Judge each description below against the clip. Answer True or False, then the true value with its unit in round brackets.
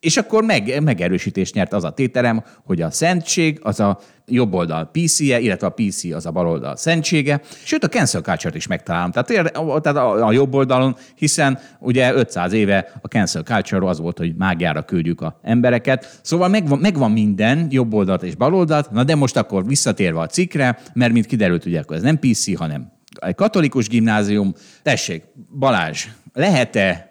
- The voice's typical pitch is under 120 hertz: False (125 Hz)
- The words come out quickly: True (170 wpm)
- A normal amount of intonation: False (7.3 semitones)